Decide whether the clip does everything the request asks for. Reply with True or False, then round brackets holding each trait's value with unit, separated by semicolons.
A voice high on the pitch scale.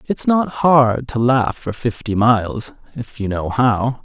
False (120 Hz)